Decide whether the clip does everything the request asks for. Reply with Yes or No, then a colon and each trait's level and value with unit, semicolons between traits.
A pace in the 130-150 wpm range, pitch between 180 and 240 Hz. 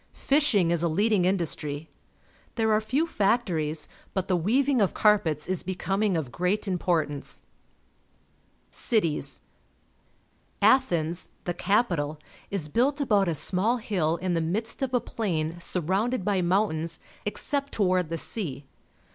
Yes: slow, 135 wpm; medium, 185 Hz